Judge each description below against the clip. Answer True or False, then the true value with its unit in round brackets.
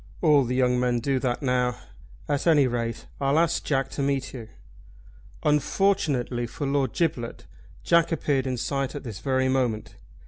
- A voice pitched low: True (130 Hz)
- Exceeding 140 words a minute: True (165 wpm)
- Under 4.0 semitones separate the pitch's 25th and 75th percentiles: True (2.6 semitones)